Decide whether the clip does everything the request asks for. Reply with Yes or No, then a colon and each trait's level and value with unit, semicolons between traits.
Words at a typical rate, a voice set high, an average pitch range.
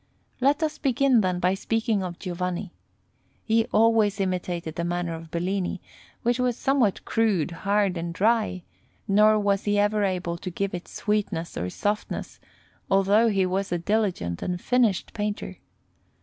Yes: average, 150 wpm; high, 200 Hz; average, 3.5 semitones